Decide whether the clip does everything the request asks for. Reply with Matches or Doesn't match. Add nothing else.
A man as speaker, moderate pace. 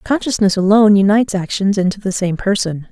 Doesn't match